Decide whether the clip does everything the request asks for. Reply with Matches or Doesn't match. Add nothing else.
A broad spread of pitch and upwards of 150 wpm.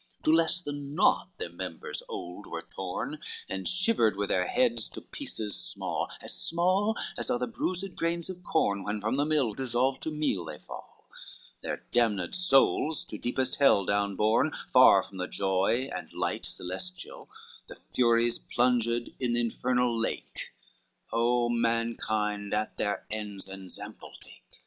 Matches